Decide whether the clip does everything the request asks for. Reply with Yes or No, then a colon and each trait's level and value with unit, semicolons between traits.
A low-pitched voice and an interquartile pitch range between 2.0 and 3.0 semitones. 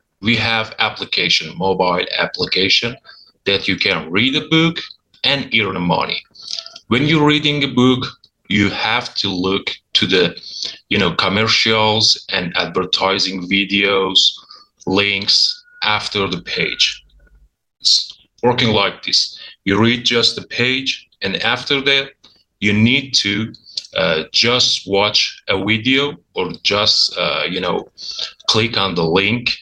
No: low, 115 Hz; average, 5.1 semitones